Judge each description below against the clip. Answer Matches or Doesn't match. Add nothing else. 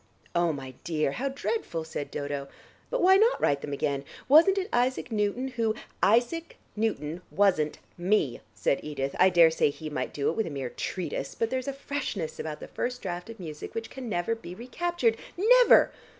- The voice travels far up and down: Matches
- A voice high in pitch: Matches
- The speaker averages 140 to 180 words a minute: Doesn't match